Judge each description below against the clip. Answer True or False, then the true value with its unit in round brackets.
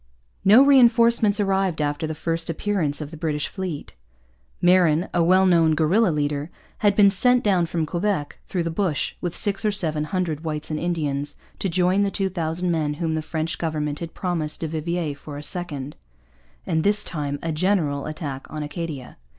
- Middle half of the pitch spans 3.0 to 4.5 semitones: True (3.7 semitones)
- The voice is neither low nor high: True (165 Hz)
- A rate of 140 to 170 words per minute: False (185 wpm)